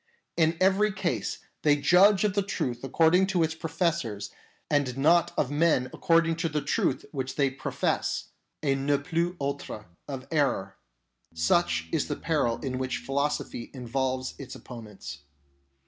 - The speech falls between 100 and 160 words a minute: Yes, average, 150 wpm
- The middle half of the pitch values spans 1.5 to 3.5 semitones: No, average, 4.3 semitones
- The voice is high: No, medium, 145 Hz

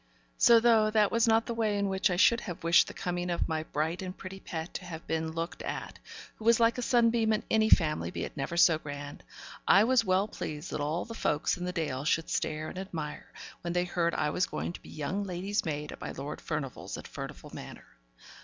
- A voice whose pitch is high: No, medium, 180 Hz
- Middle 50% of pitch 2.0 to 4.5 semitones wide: No, average, 5.1 semitones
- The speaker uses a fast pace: Yes, fast, 235 wpm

